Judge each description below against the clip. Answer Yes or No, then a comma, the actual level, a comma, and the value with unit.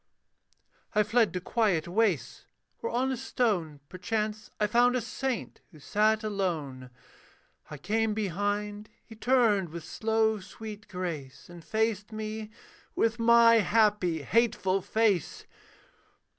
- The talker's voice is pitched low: No, high, 210 Hz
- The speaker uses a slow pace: Yes, slow, 125 wpm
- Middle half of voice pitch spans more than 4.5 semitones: No, average, 3.6 semitones